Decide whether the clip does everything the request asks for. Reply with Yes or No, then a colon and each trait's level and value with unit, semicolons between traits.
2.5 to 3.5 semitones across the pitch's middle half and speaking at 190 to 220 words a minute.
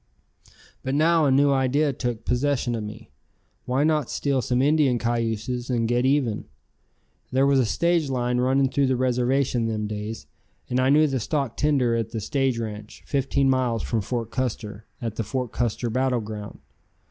No: average, 3.1 semitones; average, 175 wpm